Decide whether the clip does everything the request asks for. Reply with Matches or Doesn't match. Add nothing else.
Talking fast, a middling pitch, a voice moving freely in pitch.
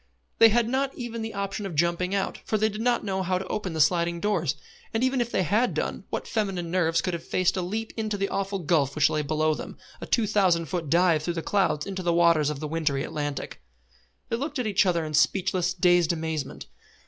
Doesn't match